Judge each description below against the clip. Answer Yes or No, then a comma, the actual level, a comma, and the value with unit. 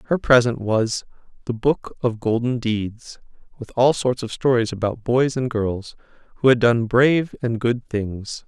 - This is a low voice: Yes, low, 120 Hz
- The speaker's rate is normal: Yes, average, 170 wpm